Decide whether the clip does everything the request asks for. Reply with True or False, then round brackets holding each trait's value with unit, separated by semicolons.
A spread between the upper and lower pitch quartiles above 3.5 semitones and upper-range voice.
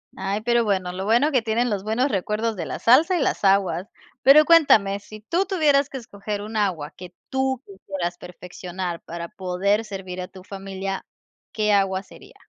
True (4.0 semitones; 200 Hz)